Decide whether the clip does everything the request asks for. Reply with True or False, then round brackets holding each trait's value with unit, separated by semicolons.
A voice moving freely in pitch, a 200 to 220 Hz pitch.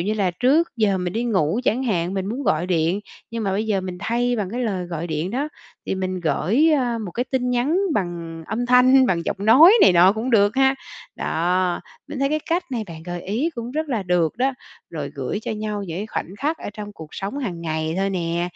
True (5.8 semitones; 205 Hz)